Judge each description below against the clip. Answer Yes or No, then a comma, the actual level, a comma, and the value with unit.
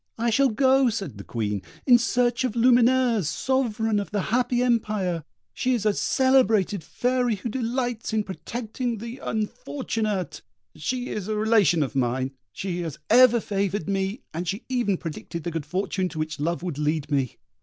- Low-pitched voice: No, high, 210 Hz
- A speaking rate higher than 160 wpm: Yes, average, 170 wpm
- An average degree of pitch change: No, wide, 5.9 semitones